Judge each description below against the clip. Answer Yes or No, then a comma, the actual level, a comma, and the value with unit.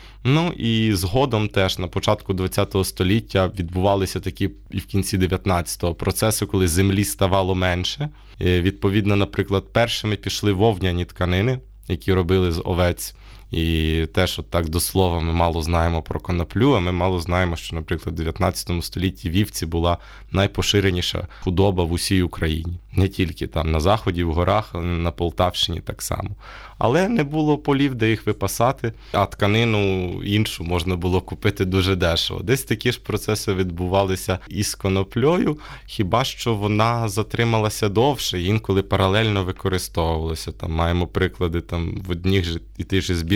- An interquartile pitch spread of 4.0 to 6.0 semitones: No, average, 2.9 semitones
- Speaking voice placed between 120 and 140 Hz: No, very low, 95 Hz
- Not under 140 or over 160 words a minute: Yes, average, 150 wpm